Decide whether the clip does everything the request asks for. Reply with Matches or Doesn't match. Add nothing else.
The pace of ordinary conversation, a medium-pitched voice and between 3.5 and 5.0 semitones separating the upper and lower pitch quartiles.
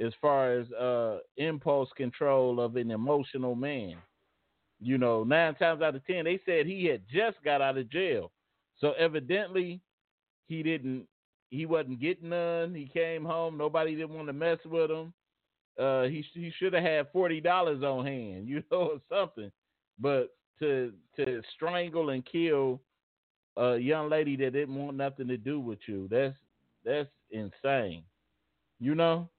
Matches